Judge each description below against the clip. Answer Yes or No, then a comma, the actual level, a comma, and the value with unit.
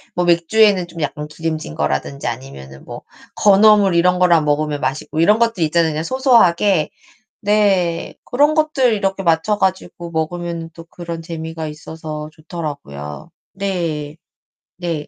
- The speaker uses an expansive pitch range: No, average, 4.0 semitones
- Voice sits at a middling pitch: Yes, medium, 170 Hz